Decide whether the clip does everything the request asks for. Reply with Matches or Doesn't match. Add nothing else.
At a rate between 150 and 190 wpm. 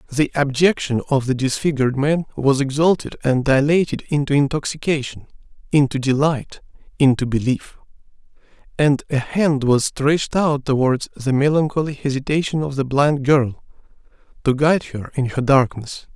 Doesn't match